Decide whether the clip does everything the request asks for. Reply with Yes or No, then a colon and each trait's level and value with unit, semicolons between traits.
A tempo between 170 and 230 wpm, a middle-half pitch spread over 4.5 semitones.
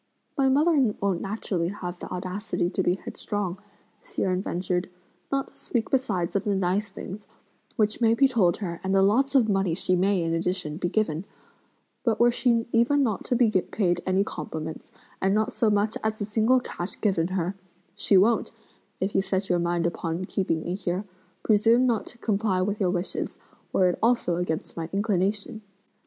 No: average, 185 wpm; average, 3.6 semitones